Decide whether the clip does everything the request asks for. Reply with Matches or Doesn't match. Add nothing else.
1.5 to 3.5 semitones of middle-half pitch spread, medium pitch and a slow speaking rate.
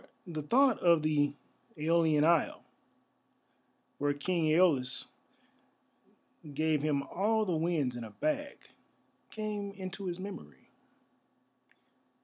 Doesn't match